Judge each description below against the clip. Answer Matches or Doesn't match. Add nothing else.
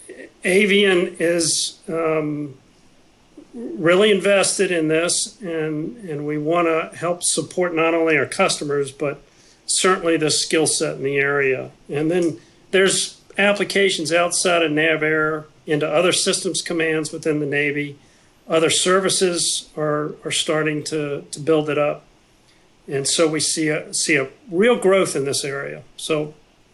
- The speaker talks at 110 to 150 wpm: Matches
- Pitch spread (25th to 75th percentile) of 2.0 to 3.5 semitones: Matches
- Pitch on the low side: Doesn't match